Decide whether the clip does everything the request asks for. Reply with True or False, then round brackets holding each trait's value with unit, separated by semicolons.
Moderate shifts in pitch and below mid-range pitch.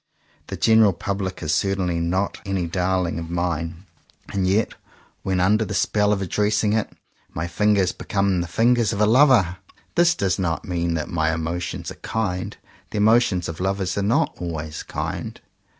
True (3.3 semitones; 95 Hz)